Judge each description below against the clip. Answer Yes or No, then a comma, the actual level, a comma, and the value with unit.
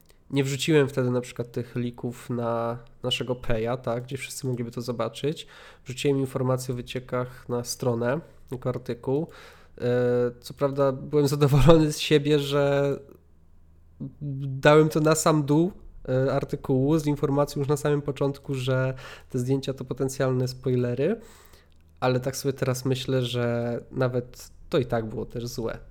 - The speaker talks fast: No, average, 145 wpm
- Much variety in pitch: No, narrow, 2.6 semitones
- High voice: No, low, 130 Hz